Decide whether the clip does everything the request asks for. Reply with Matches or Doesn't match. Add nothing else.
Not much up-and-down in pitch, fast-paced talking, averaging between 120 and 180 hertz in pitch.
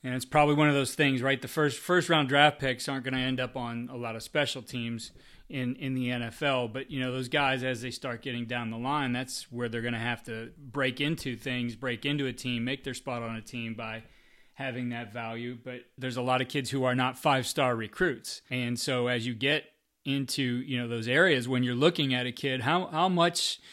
Matches